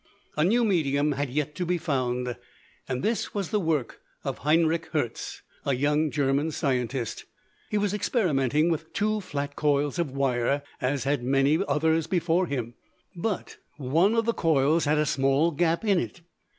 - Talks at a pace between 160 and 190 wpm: Yes, average, 165 wpm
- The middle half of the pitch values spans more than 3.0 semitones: Yes, average, 3.8 semitones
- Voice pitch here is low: No, medium, 150 Hz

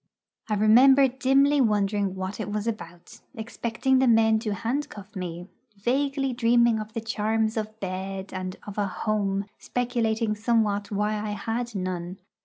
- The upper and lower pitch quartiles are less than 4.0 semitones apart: Yes, average, 3.0 semitones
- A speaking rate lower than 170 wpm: Yes, average, 150 wpm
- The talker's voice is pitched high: Yes, high, 215 Hz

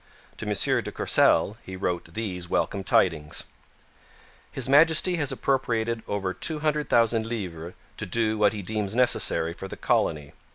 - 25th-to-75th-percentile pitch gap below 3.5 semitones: No, average, 4.4 semitones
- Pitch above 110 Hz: No, low, 105 Hz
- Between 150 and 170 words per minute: No, average, 140 wpm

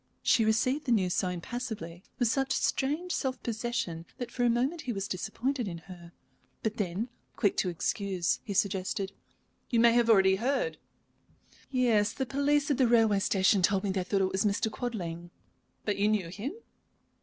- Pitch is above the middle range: Yes, high, 215 Hz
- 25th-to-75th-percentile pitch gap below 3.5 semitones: No, average, 4.4 semitones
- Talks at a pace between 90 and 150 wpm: No, average, 180 wpm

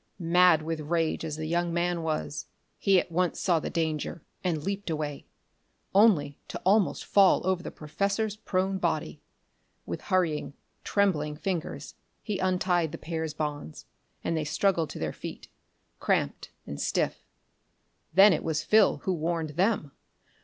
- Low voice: No, medium, 170 Hz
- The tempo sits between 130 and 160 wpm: Yes, average, 150 wpm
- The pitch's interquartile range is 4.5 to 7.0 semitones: No, average, 3.4 semitones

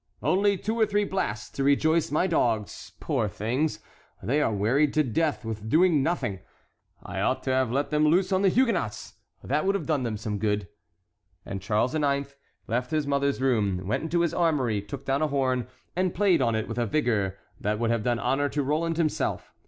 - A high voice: No, medium, 140 Hz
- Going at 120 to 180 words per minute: No, average, 200 wpm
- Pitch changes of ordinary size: No, wide, 6.4 semitones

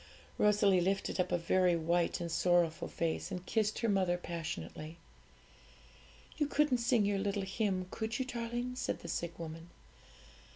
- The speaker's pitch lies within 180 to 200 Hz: Yes, medium, 185 Hz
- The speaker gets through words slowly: No, average, 155 wpm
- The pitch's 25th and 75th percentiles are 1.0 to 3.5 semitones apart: No, average, 4.4 semitones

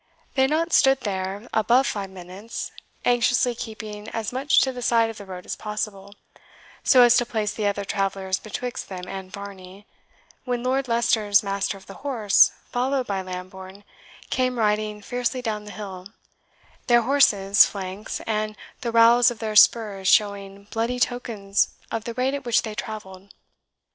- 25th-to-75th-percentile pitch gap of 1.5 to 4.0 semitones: Yes, average, 3.6 semitones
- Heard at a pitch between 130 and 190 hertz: No, high, 215 Hz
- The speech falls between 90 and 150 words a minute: No, average, 165 wpm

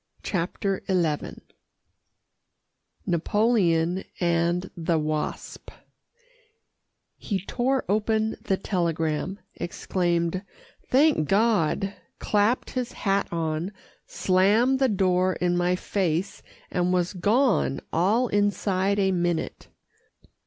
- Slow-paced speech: Yes, slow, 90 wpm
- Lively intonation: No, average, 3.2 semitones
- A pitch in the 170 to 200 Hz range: Yes, medium, 185 Hz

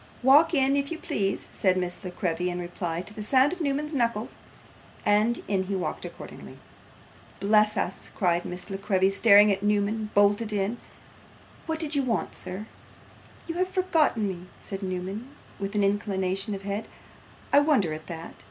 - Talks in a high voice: Yes, high, 205 Hz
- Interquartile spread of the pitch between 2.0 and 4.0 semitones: No, average, 5.2 semitones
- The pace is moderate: Yes, average, 175 wpm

